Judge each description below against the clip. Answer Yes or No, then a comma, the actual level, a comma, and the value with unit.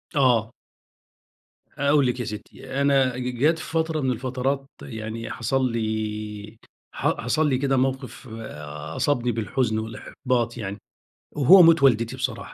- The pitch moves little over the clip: No, average, 3.4 semitones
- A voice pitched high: No, low, 125 Hz